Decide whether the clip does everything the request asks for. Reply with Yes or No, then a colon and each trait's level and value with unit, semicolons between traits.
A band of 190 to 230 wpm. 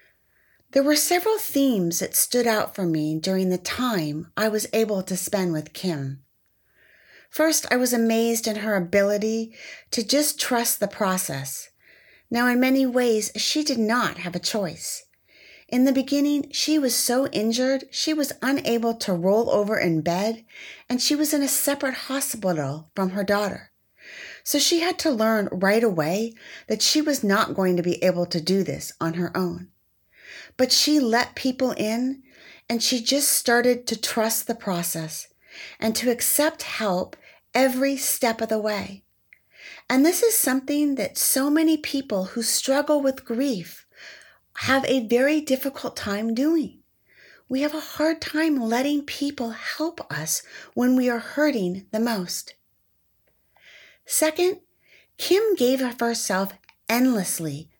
No: average, 155 wpm